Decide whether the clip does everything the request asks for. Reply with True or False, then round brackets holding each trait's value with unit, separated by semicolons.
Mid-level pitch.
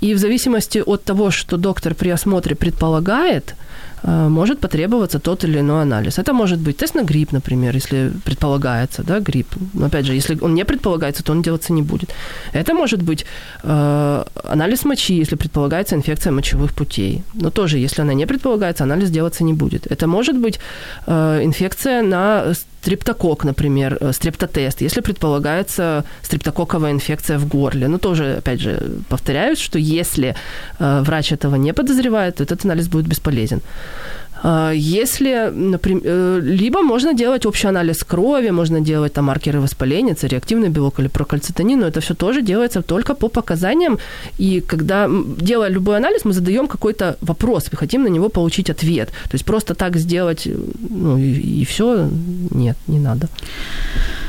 True (165 Hz)